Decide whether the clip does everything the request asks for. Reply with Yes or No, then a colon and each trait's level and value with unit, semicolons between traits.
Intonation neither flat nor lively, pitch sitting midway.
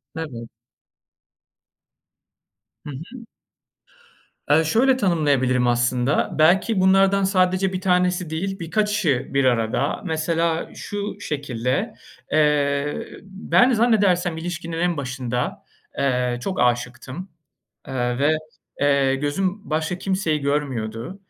No: wide, 6.0 semitones; medium, 160 Hz